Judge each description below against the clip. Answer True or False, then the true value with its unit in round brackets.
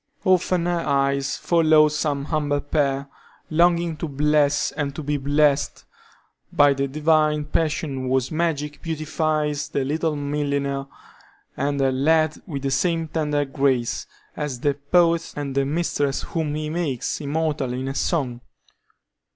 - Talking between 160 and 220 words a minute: False (140 wpm)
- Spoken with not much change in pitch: True (2.2 semitones)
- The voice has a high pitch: False (150 Hz)